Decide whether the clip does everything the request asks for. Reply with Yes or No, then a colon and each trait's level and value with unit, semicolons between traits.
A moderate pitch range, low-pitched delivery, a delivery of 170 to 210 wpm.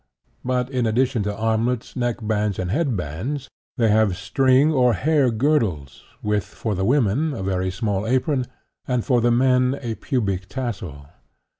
No: average, 4.0 semitones; low, 120 Hz; average, 160 wpm